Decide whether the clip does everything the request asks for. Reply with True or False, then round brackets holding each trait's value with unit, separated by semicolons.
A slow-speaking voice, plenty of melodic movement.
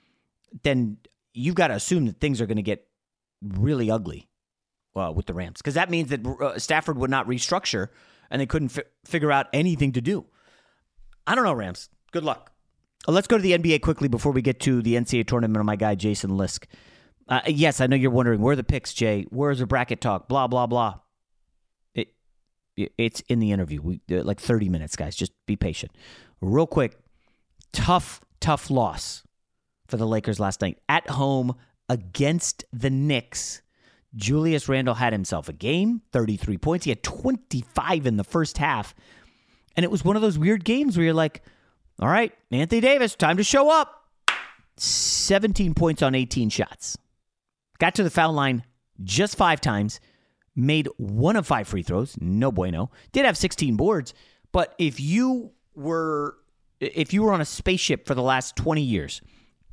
False (180 wpm; 6.8 semitones)